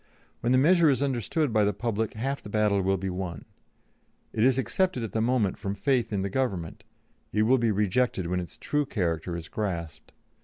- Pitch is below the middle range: Yes, low, 110 Hz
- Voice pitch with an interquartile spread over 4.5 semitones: Yes, average, 5.1 semitones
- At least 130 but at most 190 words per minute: No, average, 200 wpm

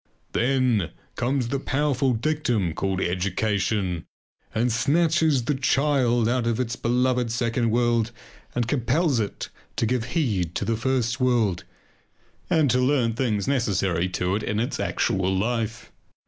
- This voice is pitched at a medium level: No, low, 120 Hz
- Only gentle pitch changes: No, average, 3.4 semitones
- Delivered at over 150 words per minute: No, average, 140 wpm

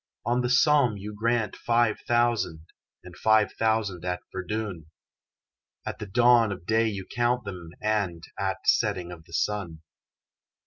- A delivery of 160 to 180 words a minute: No, average, 145 wpm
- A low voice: Yes, low, 105 Hz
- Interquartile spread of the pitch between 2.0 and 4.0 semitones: No, average, 4.6 semitones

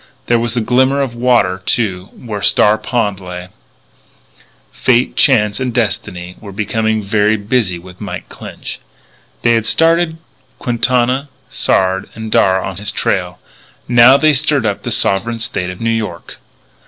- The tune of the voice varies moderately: Yes, average, 4.2 semitones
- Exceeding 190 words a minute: No, average, 150 wpm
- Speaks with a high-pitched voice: No, low, 110 Hz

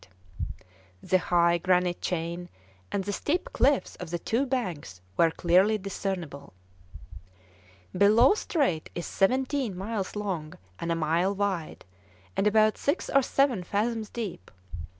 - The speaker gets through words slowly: Yes, slow, 130 wpm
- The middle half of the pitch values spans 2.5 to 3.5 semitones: No, average, 4.7 semitones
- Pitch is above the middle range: Yes, high, 195 Hz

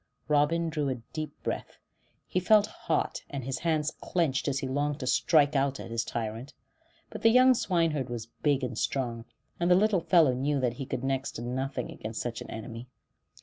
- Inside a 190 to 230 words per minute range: Yes, average, 200 wpm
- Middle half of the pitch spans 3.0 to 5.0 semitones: Yes, average, 4.5 semitones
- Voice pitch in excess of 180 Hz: No, medium, 140 Hz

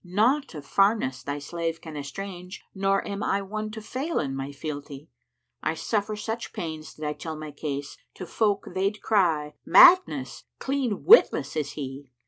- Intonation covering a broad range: Yes, wide, 6.4 semitones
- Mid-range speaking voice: Yes, medium, 175 Hz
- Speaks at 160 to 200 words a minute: Yes, average, 175 wpm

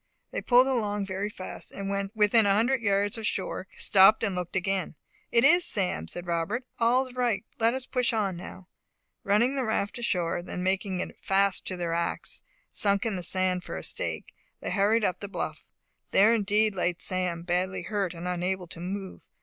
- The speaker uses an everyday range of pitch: Yes, average, 3.4 semitones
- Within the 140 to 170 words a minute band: No, average, 190 wpm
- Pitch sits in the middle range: No, high, 195 Hz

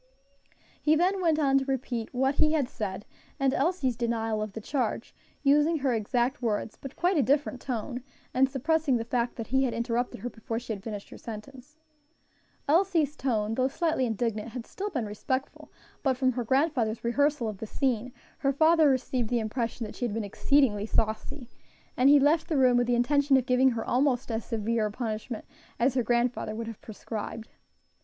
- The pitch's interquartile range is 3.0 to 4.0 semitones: Yes, average, 3.5 semitones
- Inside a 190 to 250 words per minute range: Yes, average, 195 wpm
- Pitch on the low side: No, very high, 250 Hz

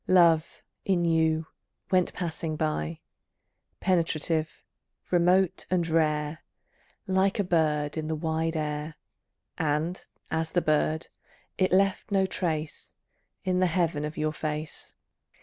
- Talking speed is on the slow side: Yes, slow, 120 wpm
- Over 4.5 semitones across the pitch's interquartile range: No, average, 2.7 semitones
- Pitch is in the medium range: Yes, medium, 160 Hz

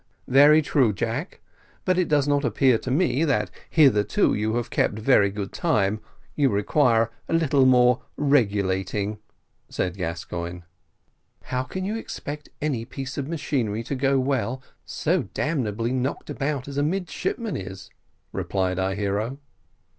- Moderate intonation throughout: No, wide, 5.8 semitones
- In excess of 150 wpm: No, average, 145 wpm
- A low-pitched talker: Yes, low, 130 Hz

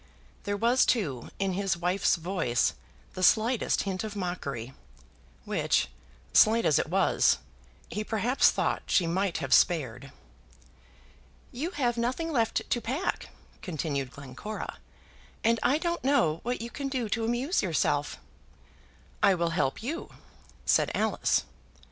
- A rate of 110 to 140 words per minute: Yes, slow, 135 wpm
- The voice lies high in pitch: Yes, high, 205 Hz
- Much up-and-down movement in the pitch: Yes, wide, 6.4 semitones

